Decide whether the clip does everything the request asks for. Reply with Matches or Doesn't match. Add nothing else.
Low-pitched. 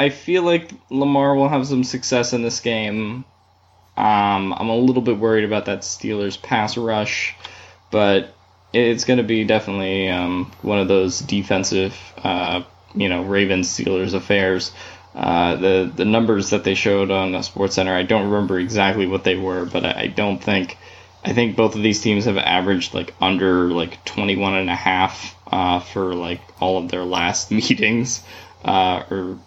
Matches